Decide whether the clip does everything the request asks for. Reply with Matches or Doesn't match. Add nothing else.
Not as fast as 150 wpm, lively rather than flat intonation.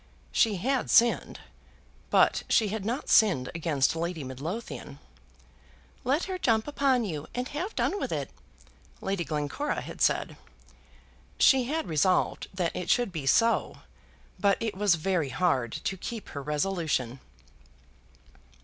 Matches